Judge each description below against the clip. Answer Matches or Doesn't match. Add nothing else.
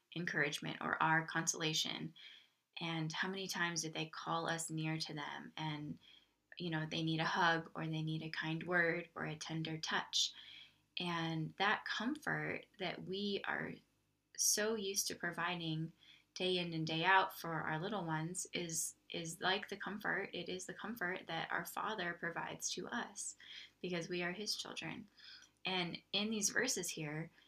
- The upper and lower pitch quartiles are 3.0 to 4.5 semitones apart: Doesn't match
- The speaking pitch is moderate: Matches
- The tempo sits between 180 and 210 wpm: Doesn't match